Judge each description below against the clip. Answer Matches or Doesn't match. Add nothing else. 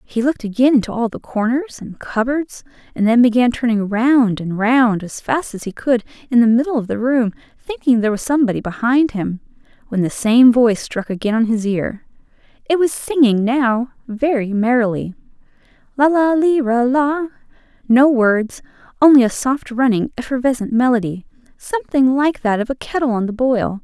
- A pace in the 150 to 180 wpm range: Matches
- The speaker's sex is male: Doesn't match